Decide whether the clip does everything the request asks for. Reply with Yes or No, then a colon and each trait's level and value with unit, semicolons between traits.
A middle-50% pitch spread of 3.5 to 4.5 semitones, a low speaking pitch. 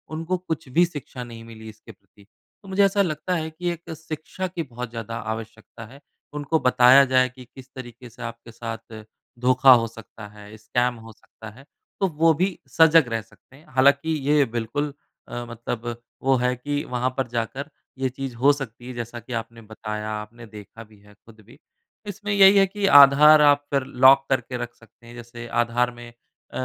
Yes: average, 4.2 semitones; low, 125 Hz